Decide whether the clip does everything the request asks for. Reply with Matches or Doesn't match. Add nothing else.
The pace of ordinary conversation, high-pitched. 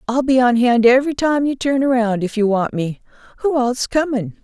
Doesn't match